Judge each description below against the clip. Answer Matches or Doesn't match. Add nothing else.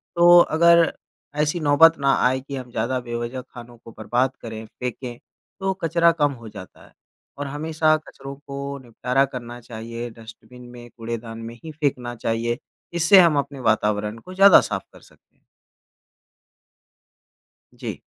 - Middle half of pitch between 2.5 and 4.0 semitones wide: Doesn't match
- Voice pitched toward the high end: Doesn't match